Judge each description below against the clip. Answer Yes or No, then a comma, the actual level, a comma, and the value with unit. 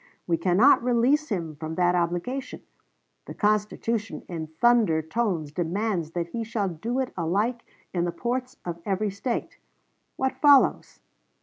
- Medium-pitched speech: No, high, 200 Hz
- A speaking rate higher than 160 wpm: No, average, 140 wpm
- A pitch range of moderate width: No, wide, 5.7 semitones